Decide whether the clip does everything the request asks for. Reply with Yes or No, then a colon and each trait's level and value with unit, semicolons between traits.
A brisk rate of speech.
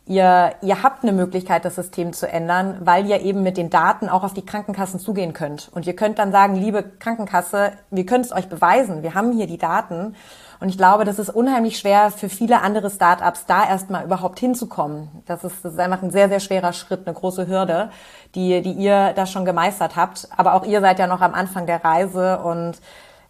Yes: fast, 220 wpm